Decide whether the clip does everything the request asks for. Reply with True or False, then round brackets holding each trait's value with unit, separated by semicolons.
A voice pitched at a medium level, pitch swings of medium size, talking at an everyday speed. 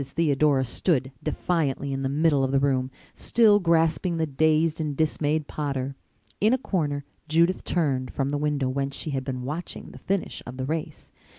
True (145 Hz; 3.2 semitones; 180 wpm)